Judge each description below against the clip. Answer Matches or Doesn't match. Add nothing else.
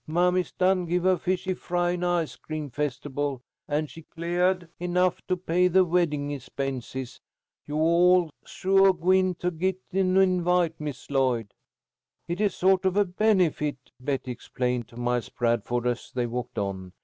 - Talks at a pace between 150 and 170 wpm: Matches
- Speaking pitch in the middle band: Matches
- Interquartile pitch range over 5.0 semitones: Matches